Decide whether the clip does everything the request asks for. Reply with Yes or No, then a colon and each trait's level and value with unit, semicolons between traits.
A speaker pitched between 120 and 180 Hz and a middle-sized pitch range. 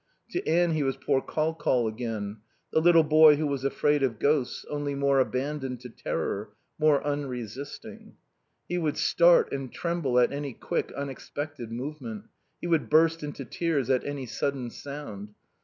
Yes: medium, 140 Hz; average, 3.5 semitones